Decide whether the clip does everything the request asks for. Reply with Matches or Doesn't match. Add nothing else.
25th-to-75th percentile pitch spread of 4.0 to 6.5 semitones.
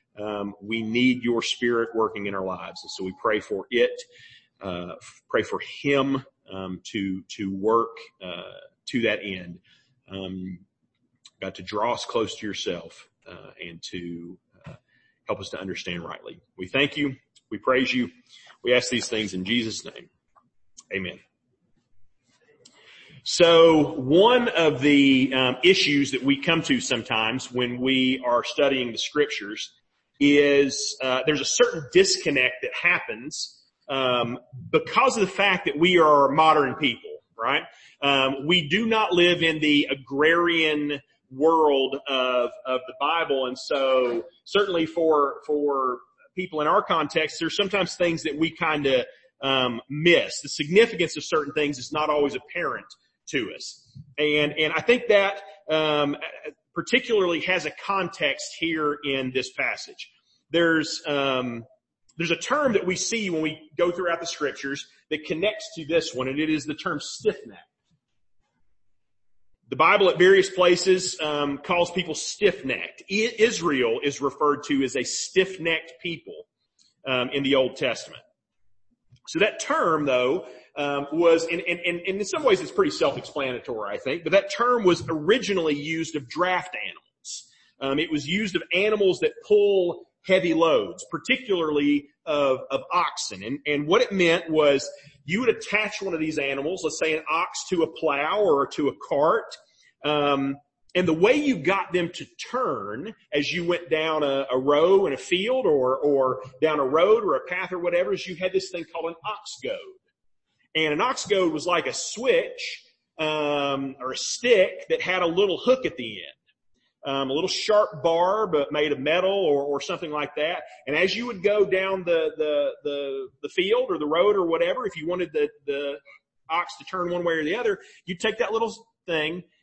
Matches